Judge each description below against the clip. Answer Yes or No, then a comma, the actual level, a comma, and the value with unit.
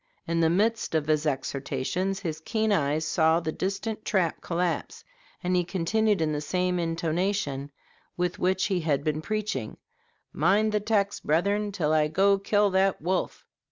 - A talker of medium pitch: Yes, medium, 180 Hz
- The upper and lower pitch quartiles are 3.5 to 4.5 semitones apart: Yes, average, 4.1 semitones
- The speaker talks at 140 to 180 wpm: Yes, average, 160 wpm